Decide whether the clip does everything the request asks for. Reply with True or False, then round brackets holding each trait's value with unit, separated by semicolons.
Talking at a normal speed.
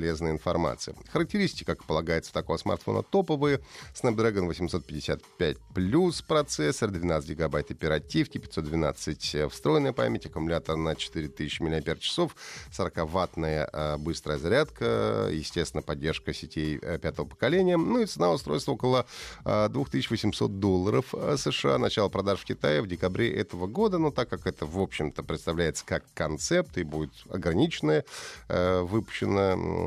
True (120 wpm)